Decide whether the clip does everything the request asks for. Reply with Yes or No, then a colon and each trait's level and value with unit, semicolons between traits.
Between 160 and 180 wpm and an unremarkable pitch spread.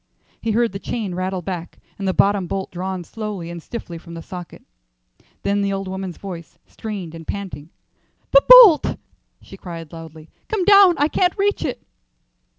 Yes: average, 170 wpm; average, 4.5 semitones